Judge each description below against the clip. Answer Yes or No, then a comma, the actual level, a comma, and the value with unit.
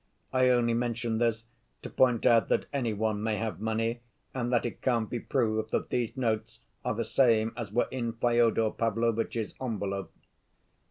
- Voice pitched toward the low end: Yes, low, 115 Hz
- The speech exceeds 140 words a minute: Yes, average, 170 wpm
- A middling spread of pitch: No, narrow, 1.6 semitones